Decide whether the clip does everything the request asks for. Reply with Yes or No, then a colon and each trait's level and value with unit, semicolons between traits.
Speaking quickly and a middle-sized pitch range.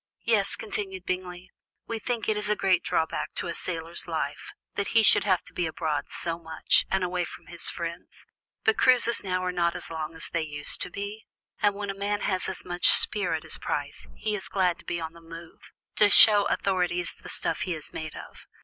Yes: fast, 210 wpm; average, 3.3 semitones